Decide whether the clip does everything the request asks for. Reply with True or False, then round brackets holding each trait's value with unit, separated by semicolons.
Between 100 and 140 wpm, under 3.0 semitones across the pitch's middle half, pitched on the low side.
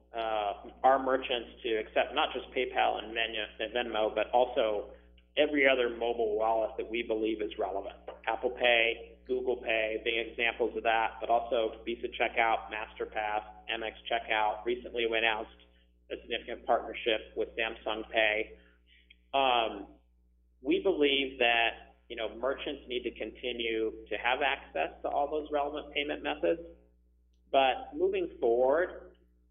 True (135 wpm; 2.6 semitones; 110 Hz)